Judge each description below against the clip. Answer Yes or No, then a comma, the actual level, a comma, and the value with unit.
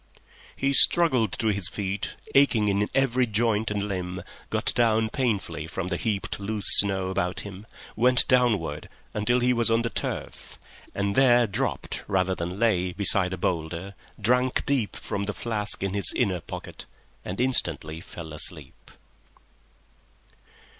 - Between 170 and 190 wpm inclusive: No, average, 145 wpm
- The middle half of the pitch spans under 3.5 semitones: No, average, 4.1 semitones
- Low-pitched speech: Yes, low, 105 Hz